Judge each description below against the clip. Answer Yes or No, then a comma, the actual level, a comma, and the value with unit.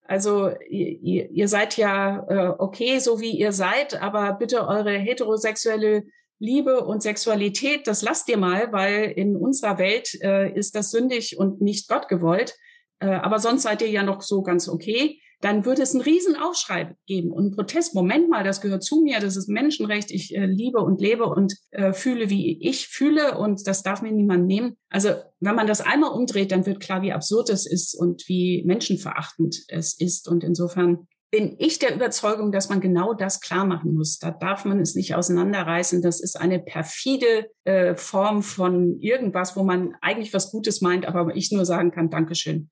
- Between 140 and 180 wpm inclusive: No, fast, 190 wpm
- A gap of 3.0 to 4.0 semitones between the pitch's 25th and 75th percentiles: Yes, average, 3.5 semitones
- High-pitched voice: Yes, high, 200 Hz